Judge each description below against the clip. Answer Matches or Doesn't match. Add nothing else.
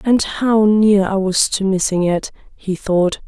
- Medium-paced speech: Matches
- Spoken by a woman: Matches